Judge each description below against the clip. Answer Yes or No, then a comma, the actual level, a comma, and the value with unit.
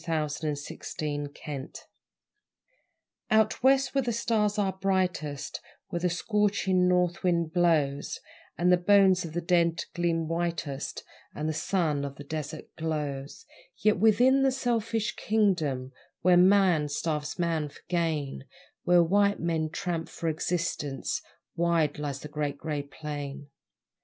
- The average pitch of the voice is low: No, medium, 170 Hz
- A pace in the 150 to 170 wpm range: No, slow, 135 wpm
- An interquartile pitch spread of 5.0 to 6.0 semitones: No, average, 4.1 semitones